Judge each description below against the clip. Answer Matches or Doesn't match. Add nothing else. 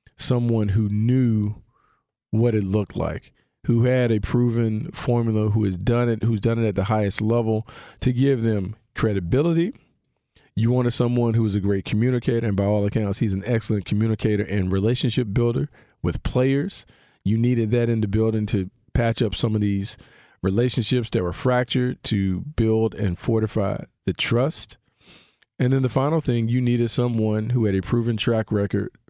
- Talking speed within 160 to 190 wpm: Matches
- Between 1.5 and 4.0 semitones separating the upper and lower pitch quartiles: Matches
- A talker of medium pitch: Doesn't match